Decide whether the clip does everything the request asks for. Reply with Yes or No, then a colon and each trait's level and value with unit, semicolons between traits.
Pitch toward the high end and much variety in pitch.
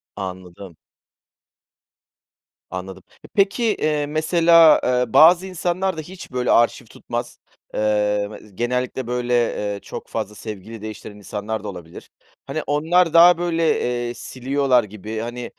No: low, 120 Hz; wide, 7.0 semitones